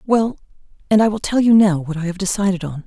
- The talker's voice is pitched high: Yes, high, 195 Hz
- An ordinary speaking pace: No, fast, 250 wpm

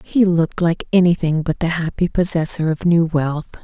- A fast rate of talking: No, average, 180 wpm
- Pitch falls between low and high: Yes, medium, 165 Hz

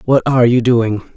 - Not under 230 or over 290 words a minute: No, fast, 205 wpm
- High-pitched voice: No, low, 120 Hz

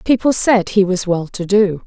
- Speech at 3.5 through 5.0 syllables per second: Yes, 4.6 syllables/s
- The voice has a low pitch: No, high, 200 Hz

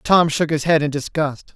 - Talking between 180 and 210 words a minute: No, fast, 230 wpm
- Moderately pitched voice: Yes, medium, 155 Hz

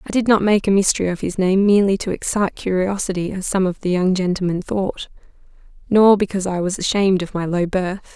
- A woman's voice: Yes, female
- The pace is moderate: No, fast, 215 wpm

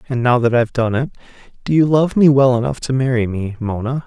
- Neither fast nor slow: No, fast, 220 wpm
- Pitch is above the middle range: No, low, 125 Hz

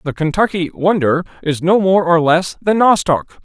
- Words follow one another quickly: No, average, 175 wpm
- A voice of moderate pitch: Yes, medium, 175 Hz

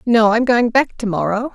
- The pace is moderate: No, fast, 235 wpm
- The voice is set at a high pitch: Yes, high, 230 Hz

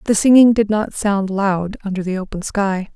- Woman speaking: Yes, female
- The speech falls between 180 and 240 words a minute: Yes, fast, 205 wpm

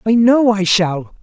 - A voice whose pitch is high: Yes, high, 210 Hz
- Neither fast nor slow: Yes, average, 195 wpm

